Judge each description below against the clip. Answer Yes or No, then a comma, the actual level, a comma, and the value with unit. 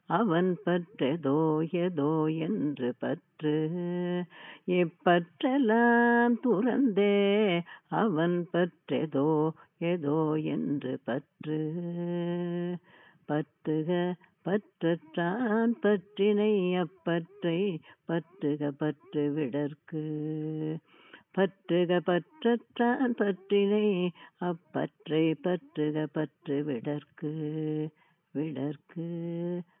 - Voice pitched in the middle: Yes, medium, 170 Hz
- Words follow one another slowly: Yes, slow, 55 wpm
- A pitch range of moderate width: Yes, average, 3.3 semitones